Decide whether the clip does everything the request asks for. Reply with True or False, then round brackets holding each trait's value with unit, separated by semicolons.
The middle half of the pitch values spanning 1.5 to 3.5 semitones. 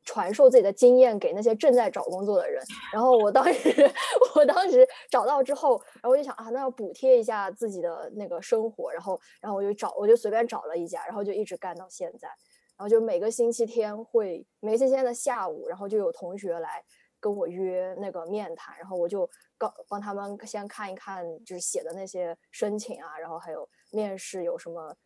False (5.5 semitones)